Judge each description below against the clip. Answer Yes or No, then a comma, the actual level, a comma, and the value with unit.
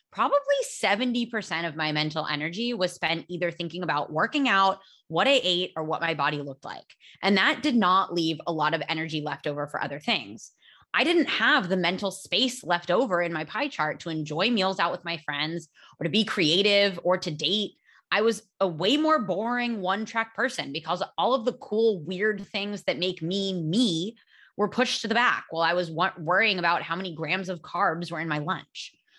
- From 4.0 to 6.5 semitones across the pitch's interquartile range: Yes, average, 5.0 semitones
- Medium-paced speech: No, fast, 210 wpm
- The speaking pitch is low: No, medium, 185 Hz